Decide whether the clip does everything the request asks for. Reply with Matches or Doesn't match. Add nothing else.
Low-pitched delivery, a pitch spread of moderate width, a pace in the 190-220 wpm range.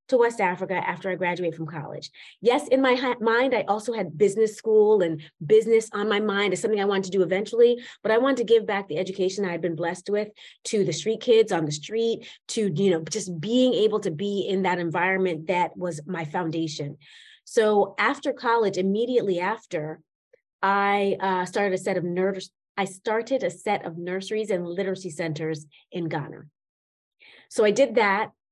Doesn't match